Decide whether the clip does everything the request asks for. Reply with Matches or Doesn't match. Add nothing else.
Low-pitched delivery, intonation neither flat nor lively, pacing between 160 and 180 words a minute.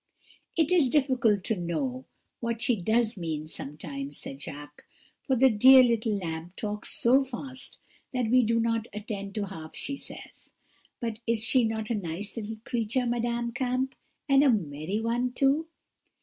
Doesn't match